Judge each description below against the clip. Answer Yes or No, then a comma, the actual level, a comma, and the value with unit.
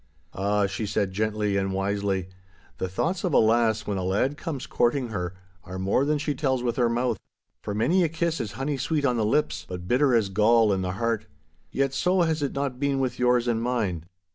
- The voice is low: Yes, low, 115 Hz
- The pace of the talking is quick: Yes, fast, 215 wpm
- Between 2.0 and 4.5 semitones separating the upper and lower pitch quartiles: No, wide, 5.5 semitones